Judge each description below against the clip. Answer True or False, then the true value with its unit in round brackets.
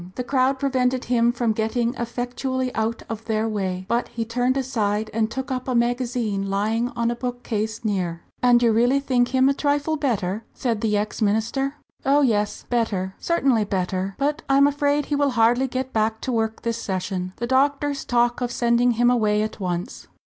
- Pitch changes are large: False (3.1 semitones)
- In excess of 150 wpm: True (190 wpm)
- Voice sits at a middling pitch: False (235 Hz)